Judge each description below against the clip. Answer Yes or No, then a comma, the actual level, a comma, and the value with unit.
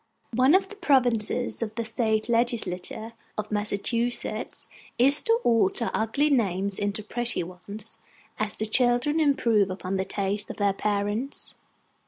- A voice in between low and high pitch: No, high, 220 Hz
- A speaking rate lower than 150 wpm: Yes, average, 140 wpm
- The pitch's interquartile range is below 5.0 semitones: Yes, average, 3.2 semitones